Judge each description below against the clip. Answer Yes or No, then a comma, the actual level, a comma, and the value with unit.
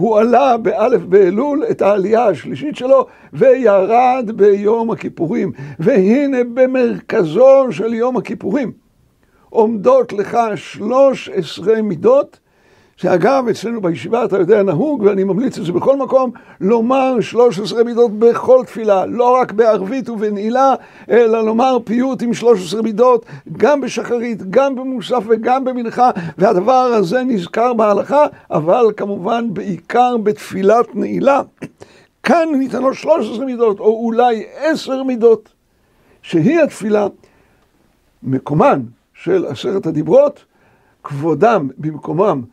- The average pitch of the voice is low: No, high, 230 Hz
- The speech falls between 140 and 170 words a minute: No, average, 110 wpm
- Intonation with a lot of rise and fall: No, average, 4.0 semitones